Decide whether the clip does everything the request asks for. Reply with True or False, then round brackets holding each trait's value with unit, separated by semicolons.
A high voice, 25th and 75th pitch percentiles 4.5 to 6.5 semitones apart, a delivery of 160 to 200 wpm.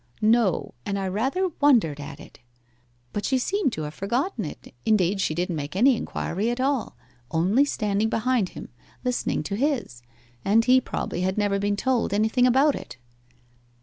True (215 Hz; 5.1 semitones; 170 wpm)